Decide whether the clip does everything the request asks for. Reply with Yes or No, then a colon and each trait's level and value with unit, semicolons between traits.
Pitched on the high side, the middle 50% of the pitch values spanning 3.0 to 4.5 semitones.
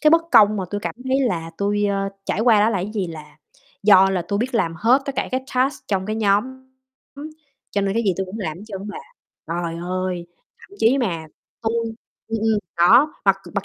Yes: high, 205 Hz; average, 3.5 semitones